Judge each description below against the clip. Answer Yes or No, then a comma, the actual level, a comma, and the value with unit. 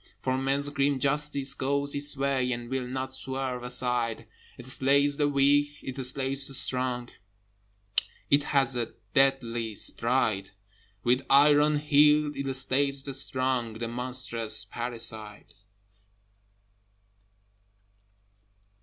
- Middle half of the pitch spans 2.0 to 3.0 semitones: Yes, narrow, 2.4 semitones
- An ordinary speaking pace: No, slow, 110 wpm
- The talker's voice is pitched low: Yes, low, 130 Hz